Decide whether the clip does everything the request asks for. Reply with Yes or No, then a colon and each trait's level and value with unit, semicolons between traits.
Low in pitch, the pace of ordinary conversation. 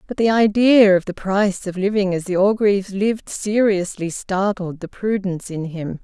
No: high, 195 Hz; average, 180 wpm